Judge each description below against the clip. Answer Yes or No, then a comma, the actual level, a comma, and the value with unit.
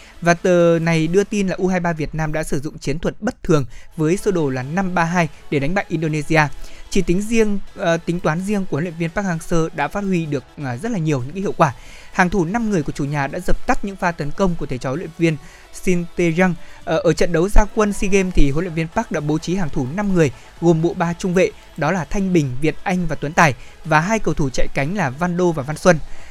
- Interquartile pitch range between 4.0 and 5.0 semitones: No, average, 3.6 semitones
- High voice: No, medium, 170 Hz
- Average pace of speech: No, fast, 265 wpm